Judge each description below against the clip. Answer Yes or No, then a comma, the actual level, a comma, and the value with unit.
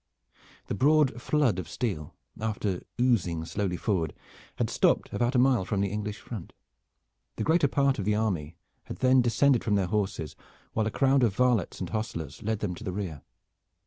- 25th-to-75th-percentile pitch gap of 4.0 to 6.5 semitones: Yes, average, 5.1 semitones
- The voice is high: No, low, 105 Hz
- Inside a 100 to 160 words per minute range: No, average, 180 wpm